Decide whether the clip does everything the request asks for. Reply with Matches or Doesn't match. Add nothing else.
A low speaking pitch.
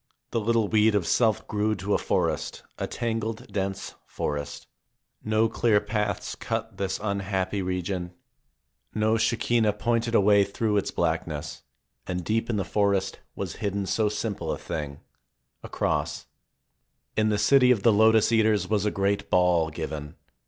Matches